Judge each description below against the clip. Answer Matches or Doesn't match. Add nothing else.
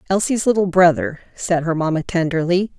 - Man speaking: Doesn't match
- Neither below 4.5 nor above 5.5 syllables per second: Matches